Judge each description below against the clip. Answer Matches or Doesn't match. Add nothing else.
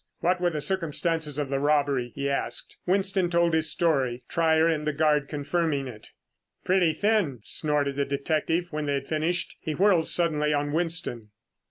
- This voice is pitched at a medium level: Matches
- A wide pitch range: Doesn't match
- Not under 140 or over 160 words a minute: Doesn't match